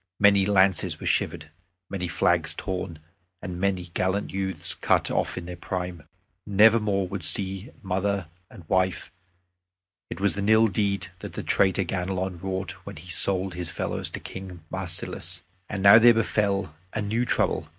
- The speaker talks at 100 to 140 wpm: No, average, 165 wpm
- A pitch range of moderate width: No, narrow, 1.9 semitones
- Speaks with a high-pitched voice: No, very low, 95 Hz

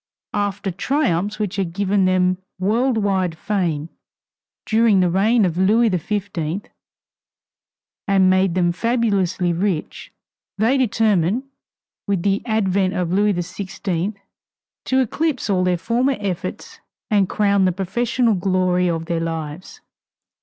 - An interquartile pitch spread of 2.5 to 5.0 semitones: Yes, average, 2.8 semitones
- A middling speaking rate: No, slow, 125 wpm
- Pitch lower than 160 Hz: No, high, 195 Hz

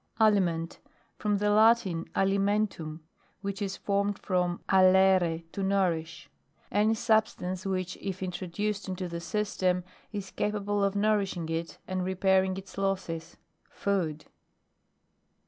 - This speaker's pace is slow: Yes, slow, 125 wpm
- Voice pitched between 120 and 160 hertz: No, high, 190 Hz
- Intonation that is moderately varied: No, narrow, 2.3 semitones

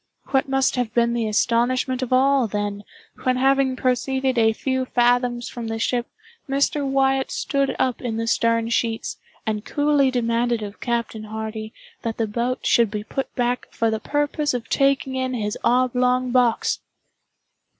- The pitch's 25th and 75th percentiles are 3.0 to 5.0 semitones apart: No, narrow, 2.4 semitones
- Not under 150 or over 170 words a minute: Yes, average, 160 wpm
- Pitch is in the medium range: No, high, 245 Hz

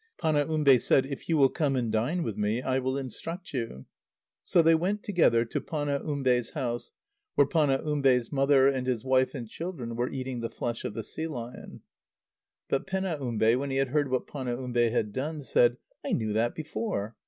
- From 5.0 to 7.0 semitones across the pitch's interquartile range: No, average, 3.8 semitones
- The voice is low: Yes, low, 130 Hz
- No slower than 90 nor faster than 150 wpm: No, average, 180 wpm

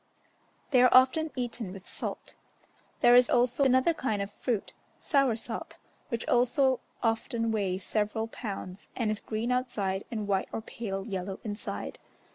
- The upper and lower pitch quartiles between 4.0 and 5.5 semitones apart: No, average, 3.5 semitones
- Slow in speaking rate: No, average, 145 wpm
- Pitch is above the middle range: Yes, high, 225 Hz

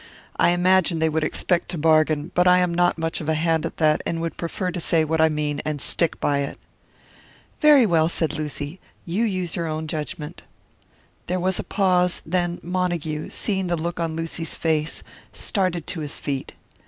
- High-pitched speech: No, medium, 165 Hz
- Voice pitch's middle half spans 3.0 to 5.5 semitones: No, narrow, 2.4 semitones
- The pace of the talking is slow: No, average, 190 wpm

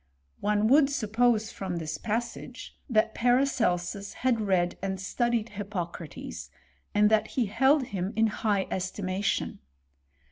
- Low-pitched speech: No, high, 210 Hz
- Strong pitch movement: No, average, 3.8 semitones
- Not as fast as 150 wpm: Yes, slow, 135 wpm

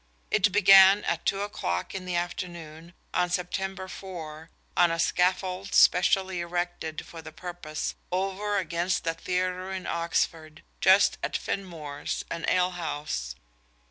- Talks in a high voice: No, medium, 180 Hz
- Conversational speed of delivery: No, slow, 130 wpm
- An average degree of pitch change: No, narrow, 2.3 semitones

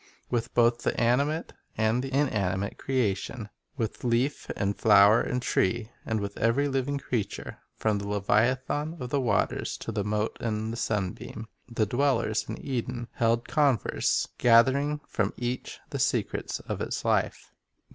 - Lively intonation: No, average, 3.5 semitones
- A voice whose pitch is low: Yes, low, 115 Hz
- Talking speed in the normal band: Yes, average, 155 wpm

